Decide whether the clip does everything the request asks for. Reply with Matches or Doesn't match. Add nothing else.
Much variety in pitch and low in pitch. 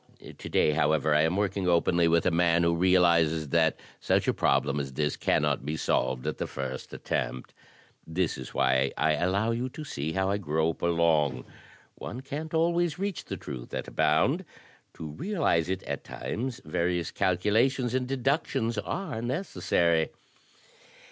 Matches